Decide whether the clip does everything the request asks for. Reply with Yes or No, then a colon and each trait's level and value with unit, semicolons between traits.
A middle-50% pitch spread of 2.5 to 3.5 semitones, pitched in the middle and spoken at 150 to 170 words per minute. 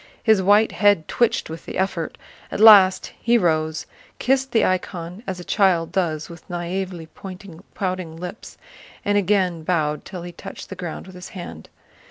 Yes: average, 3.1 semitones; medium, 180 Hz; average, 165 wpm